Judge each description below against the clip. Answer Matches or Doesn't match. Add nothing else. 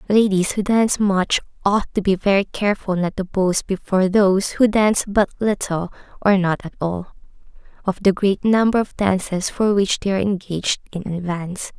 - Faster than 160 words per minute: Matches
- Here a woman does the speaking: Matches